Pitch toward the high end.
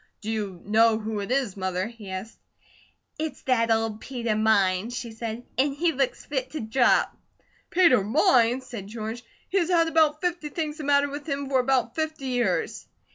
Yes: high, 245 Hz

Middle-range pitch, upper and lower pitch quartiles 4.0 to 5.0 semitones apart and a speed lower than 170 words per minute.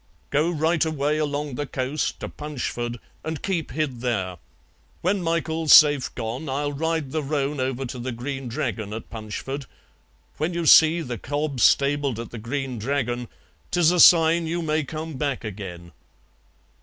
Yes: medium, 145 Hz; average, 4.4 semitones; average, 160 wpm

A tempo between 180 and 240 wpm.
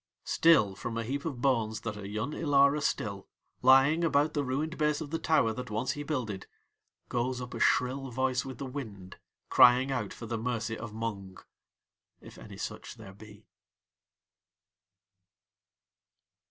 No: average, 155 wpm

